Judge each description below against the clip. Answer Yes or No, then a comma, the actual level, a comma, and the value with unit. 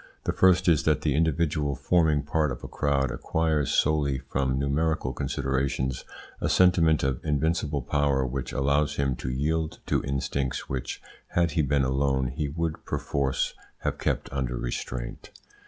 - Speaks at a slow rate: No, average, 155 wpm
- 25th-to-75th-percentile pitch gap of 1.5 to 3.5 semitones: Yes, average, 2.8 semitones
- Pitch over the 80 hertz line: No, very low, 70 Hz